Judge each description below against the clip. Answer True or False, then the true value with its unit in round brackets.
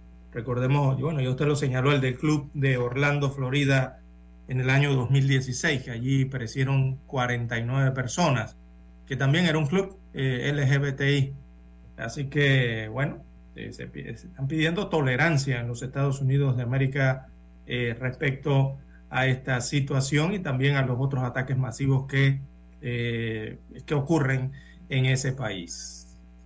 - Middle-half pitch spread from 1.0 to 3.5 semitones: True (2.4 semitones)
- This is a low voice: True (130 Hz)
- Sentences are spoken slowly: False (145 wpm)